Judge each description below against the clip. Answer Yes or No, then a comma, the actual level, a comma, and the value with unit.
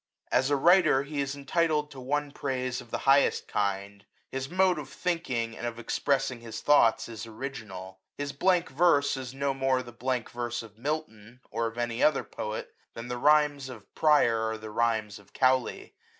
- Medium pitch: No, low, 130 Hz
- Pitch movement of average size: Yes, average, 3.9 semitones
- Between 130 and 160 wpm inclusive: No, average, 185 wpm